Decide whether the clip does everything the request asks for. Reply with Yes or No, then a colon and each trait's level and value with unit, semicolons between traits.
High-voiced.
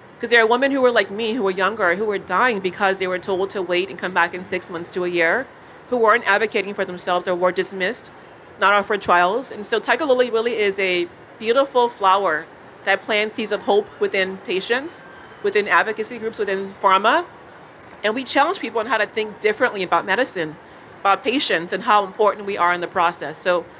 Yes: high, 200 Hz